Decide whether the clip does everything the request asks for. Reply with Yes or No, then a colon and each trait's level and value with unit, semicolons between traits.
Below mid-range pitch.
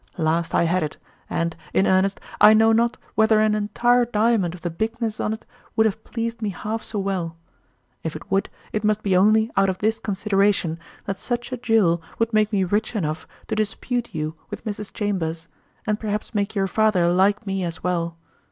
No: high, 205 Hz